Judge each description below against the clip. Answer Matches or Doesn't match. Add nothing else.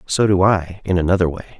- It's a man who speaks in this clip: Matches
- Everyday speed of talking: Doesn't match